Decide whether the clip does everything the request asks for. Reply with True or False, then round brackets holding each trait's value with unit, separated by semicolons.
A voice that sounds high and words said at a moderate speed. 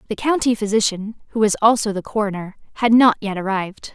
True (210 Hz; 185 wpm)